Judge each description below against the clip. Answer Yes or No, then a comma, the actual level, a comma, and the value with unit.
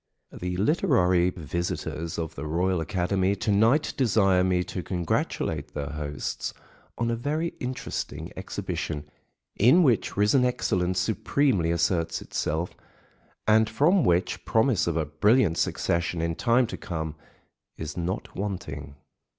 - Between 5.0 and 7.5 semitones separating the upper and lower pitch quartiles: Yes, average, 5.3 semitones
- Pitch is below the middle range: Yes, very low, 90 Hz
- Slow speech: Yes, slow, 130 wpm